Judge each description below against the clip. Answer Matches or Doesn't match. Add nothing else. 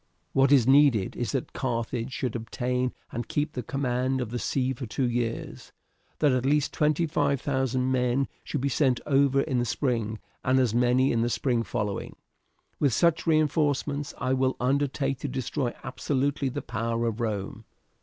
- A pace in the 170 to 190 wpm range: Matches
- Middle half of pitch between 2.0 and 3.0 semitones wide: Matches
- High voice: Doesn't match